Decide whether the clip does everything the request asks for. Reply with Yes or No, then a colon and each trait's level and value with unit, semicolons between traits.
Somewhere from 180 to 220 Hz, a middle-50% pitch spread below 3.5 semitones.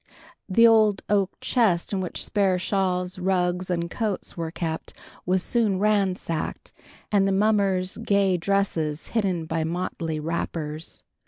Yes: medium, 185 Hz; average, 2.8 semitones